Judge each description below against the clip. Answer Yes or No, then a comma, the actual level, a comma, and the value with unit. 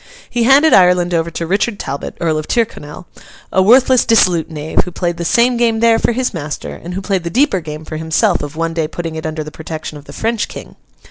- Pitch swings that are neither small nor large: No, wide, 6.2 semitones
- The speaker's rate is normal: No, fast, 230 wpm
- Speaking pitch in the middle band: Yes, medium, 175 Hz